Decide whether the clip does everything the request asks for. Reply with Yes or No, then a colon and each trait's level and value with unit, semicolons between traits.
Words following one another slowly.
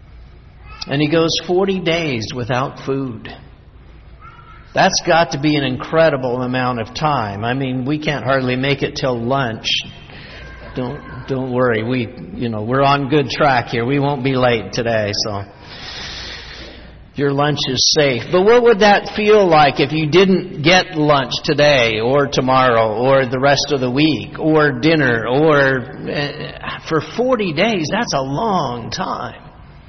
No: average, 155 wpm